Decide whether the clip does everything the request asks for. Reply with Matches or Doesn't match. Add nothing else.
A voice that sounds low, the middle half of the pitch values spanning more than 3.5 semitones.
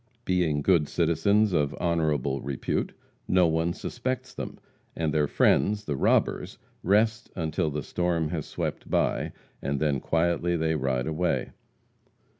Doesn't match